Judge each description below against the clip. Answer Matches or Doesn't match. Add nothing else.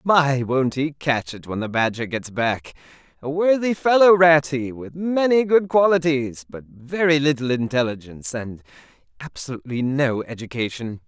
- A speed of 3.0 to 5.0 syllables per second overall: Matches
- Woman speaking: Doesn't match